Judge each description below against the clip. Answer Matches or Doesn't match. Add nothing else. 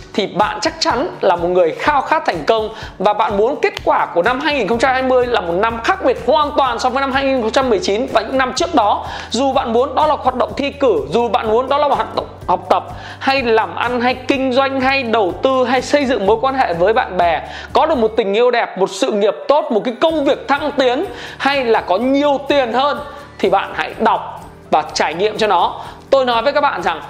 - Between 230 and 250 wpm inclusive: Matches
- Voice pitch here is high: Matches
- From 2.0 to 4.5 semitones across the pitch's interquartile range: Matches